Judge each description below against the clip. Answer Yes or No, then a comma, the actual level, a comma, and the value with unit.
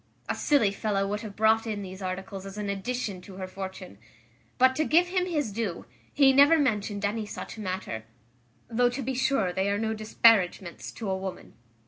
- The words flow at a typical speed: Yes, average, 190 wpm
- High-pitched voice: Yes, high, 210 Hz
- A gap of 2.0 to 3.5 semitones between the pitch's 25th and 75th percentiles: No, average, 4.2 semitones